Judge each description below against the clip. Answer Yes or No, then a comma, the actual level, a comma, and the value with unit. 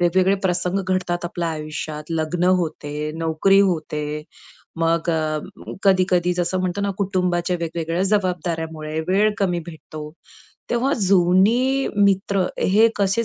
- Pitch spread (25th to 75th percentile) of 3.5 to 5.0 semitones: No, average, 3.1 semitones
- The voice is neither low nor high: Yes, medium, 175 Hz